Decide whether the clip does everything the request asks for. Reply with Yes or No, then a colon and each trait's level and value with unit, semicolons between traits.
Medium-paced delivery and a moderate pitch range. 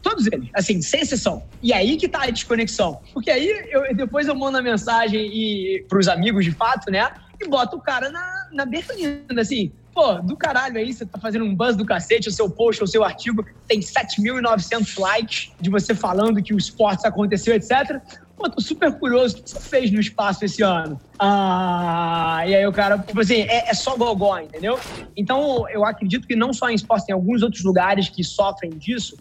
No: fast, 205 wpm; average, 4.0 semitones